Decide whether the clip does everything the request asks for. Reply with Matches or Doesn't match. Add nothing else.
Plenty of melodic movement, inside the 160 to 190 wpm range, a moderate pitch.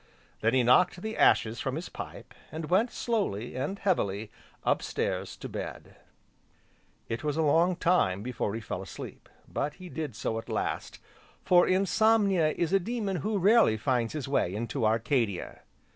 Matches